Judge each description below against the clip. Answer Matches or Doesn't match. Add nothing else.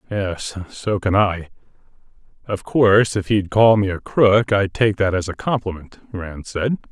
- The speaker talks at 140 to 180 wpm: Matches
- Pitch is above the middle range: Doesn't match